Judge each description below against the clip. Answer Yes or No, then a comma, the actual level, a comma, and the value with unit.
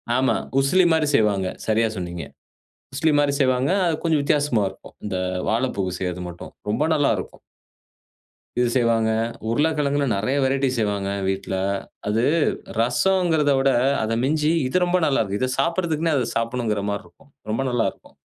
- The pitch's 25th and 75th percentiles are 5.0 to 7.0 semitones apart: Yes, wide, 5.5 semitones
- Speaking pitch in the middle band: No, low, 130 Hz